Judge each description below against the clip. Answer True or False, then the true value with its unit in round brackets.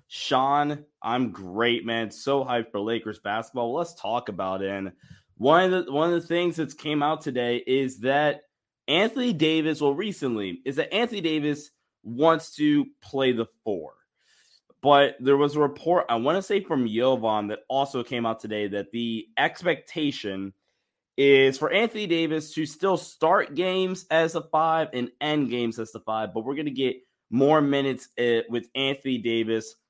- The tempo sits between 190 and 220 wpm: False (175 wpm)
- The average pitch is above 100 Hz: True (140 Hz)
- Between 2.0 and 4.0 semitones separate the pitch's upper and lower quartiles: False (5.3 semitones)